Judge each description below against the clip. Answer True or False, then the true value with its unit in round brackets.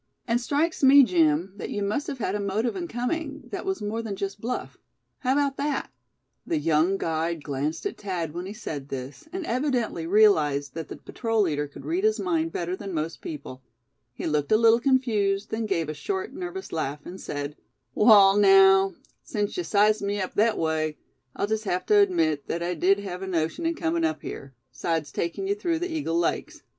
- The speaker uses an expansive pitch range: True (7.5 semitones)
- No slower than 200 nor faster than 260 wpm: True (205 wpm)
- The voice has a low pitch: False (200 Hz)